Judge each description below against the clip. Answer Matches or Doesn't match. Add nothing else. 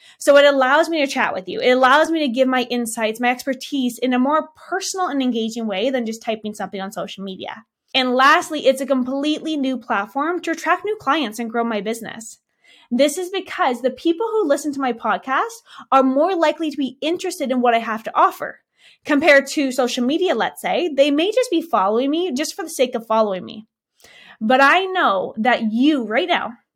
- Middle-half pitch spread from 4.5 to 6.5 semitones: Matches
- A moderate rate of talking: Doesn't match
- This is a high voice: Matches